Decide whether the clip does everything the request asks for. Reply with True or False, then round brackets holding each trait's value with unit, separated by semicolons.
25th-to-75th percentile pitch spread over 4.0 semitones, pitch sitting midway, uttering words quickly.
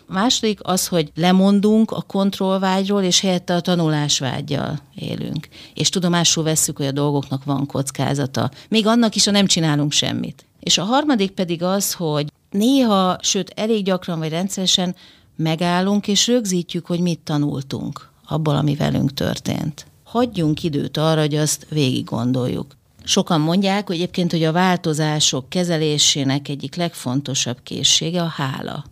False (4.5 semitones; 170 Hz; 145 wpm)